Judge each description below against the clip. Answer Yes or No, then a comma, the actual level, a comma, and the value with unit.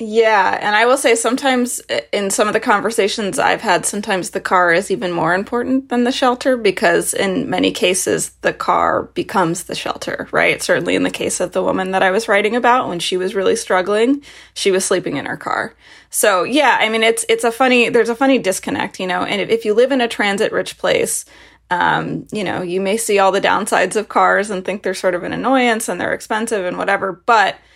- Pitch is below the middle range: No, high, 215 Hz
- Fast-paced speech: Yes, fast, 225 wpm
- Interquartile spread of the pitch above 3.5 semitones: Yes, average, 3.9 semitones